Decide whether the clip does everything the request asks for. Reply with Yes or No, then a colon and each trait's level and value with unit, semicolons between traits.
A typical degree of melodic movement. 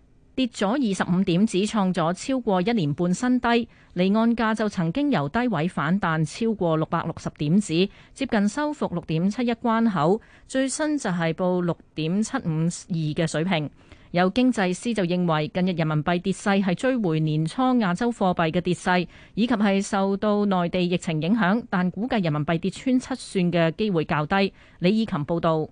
Yes: average, 5.0 semitones